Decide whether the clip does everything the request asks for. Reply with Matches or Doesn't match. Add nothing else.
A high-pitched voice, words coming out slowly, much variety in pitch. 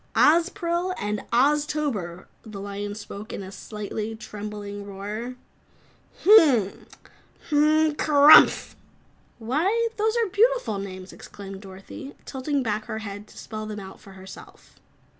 Matches